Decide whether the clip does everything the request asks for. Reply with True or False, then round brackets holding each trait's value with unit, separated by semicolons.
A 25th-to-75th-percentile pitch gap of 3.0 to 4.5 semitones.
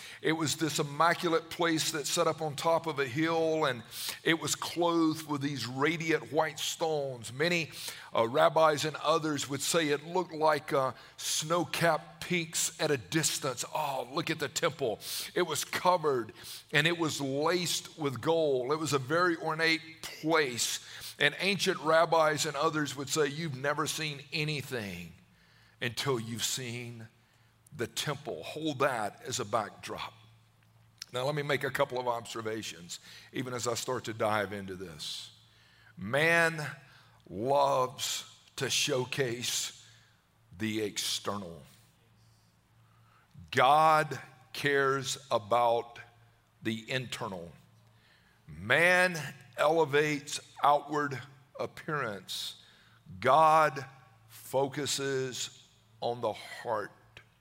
False (5.2 semitones)